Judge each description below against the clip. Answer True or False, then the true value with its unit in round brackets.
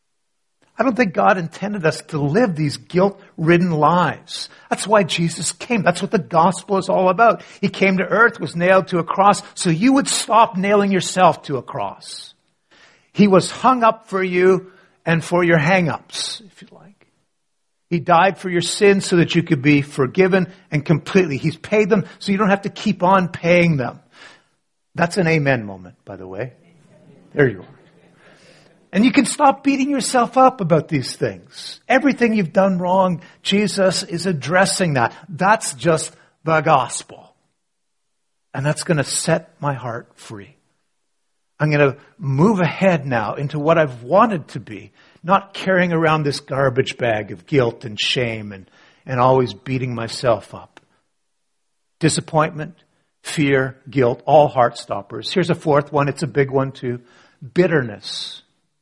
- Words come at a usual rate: True (165 wpm)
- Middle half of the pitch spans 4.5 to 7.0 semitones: True (5.1 semitones)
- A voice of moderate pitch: True (170 Hz)